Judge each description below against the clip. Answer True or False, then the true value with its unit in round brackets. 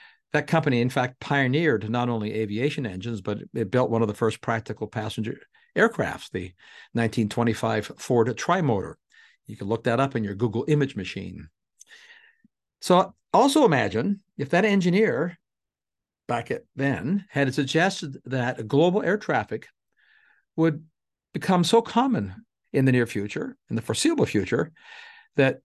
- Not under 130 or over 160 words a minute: True (145 wpm)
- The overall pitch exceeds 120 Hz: True (135 Hz)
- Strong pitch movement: True (8.3 semitones)